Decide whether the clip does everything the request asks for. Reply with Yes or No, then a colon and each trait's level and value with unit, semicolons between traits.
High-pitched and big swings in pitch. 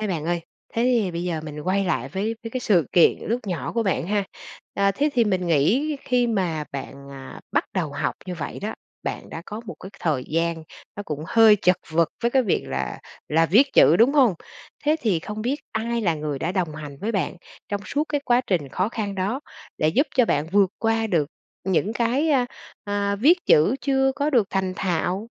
Yes: high, 200 Hz; wide, 5.9 semitones